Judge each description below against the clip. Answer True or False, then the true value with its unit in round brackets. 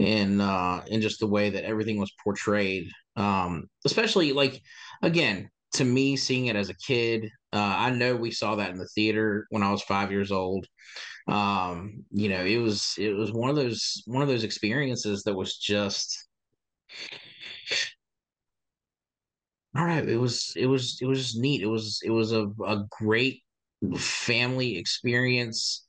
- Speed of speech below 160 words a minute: False (165 wpm)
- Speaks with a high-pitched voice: False (110 Hz)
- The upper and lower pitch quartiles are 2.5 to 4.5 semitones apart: True (3.4 semitones)